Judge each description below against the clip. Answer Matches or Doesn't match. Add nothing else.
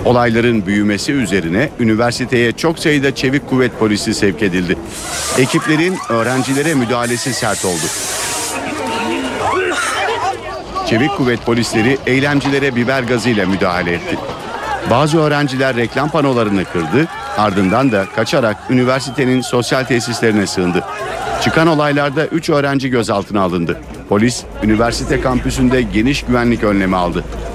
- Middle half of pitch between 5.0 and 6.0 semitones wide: Doesn't match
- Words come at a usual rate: Matches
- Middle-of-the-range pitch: Doesn't match